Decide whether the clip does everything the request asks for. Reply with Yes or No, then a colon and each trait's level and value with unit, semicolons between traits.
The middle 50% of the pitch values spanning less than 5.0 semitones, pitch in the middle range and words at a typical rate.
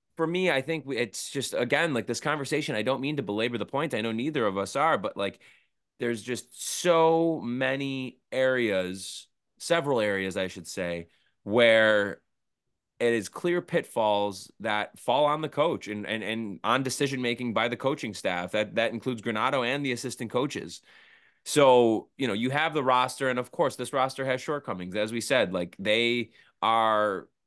No: average, 3.9 semitones; low, 120 Hz; average, 180 wpm